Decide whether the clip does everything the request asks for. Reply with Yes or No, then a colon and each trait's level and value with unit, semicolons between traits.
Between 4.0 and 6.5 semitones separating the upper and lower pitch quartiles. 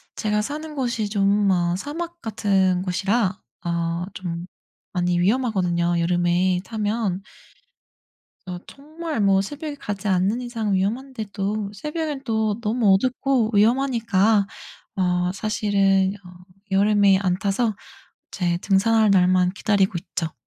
No: average, 3.6 semitones